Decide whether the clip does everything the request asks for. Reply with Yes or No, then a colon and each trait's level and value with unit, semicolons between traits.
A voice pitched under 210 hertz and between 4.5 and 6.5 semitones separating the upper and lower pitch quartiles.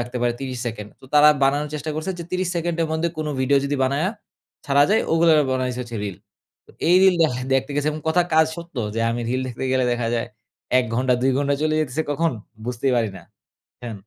No: medium, 140 Hz; average, 4.1 semitones